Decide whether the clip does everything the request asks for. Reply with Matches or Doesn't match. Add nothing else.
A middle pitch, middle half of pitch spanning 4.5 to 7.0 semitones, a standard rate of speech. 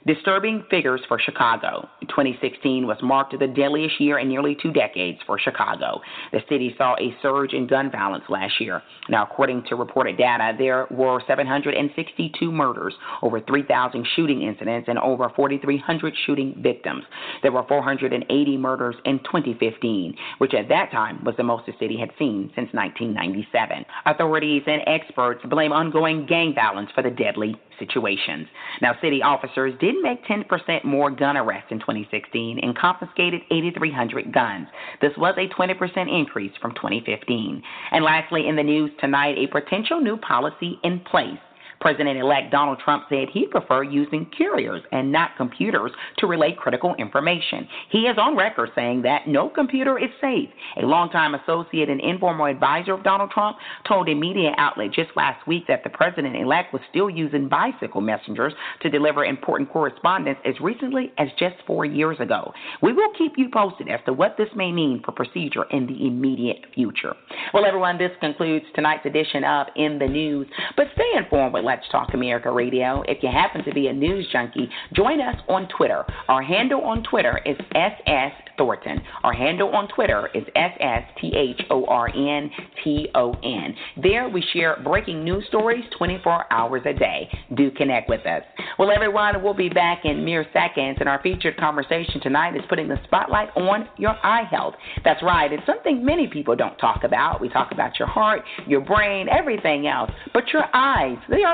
Matches